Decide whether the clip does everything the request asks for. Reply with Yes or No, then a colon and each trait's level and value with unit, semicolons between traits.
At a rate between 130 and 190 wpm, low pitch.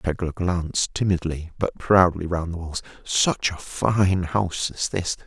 Yes: average, 150 wpm; very low, 85 Hz